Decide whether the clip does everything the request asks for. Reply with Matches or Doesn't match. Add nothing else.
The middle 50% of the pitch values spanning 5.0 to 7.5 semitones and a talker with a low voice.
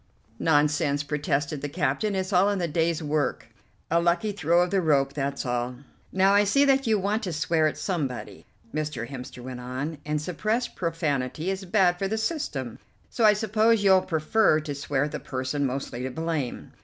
Doesn't match